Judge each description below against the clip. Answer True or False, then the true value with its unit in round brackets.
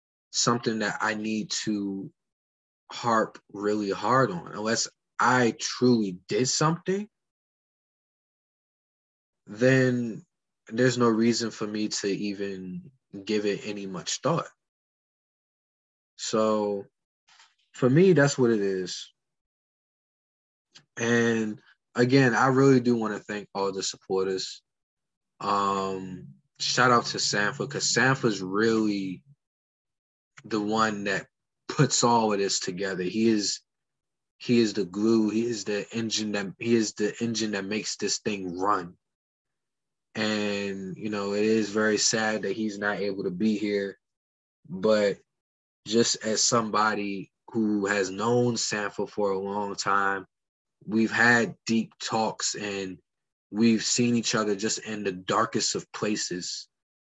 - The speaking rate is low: True (130 wpm)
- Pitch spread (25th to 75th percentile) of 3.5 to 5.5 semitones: False (2.7 semitones)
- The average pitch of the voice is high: False (105 Hz)